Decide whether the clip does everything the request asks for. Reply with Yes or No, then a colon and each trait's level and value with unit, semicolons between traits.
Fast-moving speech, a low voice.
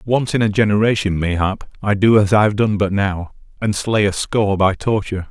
Yes: fast, 215 wpm; low, 100 Hz